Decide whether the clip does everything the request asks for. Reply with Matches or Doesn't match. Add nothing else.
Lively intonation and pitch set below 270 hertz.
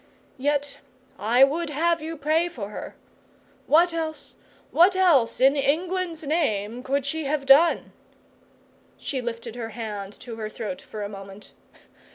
Doesn't match